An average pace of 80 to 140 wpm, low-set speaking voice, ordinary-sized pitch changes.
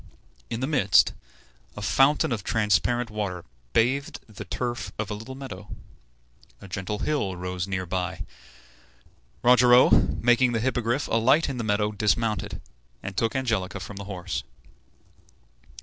Yes: slow, 135 wpm; low, 110 Hz; average, 4.1 semitones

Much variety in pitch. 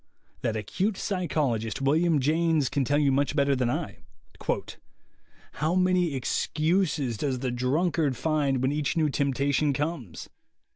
No: average, 3.6 semitones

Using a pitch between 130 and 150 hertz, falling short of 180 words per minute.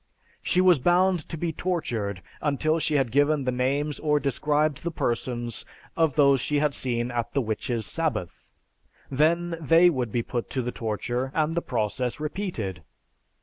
Yes: medium, 140 Hz; average, 165 wpm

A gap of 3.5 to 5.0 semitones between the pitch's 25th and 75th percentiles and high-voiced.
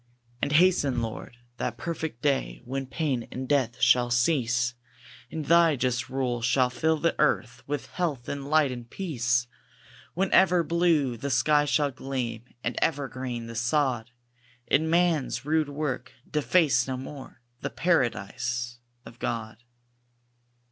No: average, 4.1 semitones; low, 130 Hz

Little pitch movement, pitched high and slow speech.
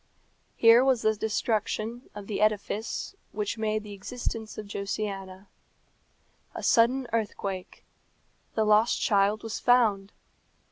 Yes: narrow, 2.0 semitones; high, 215 Hz; slow, 120 wpm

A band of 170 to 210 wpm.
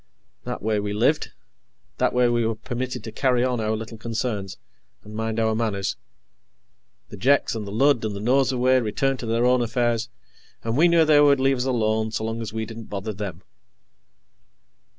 Yes: average, 190 wpm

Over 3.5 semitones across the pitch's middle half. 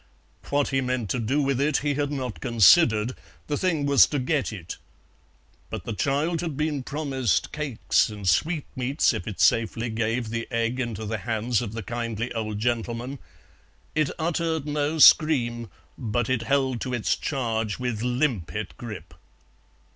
Yes: average, 4.2 semitones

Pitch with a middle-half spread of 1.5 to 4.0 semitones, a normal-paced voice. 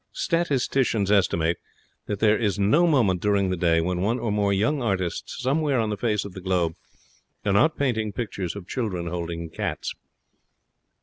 No: average, 4.6 semitones; average, 170 wpm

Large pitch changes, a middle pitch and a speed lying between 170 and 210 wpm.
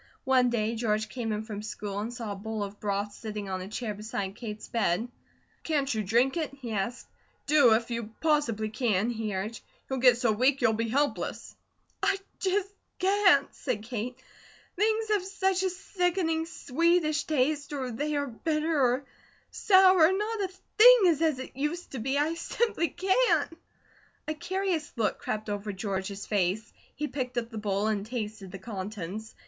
No: wide, 6.9 semitones; high, 245 Hz; average, 175 wpm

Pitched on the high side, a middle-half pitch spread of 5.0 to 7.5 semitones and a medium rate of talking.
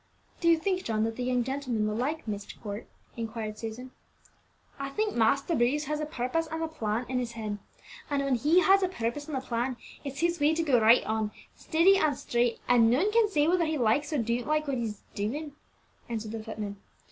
No: very high, 255 Hz; wide, 5.4 semitones; fast, 220 wpm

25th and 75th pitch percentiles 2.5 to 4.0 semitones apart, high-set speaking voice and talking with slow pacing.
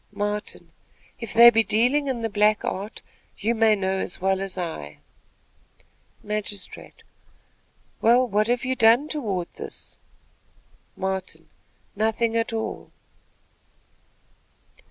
Yes: average, 3.2 semitones; high, 215 Hz; slow, 115 wpm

